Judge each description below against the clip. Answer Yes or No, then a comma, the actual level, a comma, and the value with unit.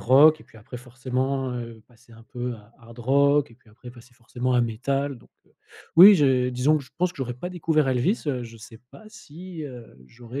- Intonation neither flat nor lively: Yes, average, 3.1 semitones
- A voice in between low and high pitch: No, low, 125 Hz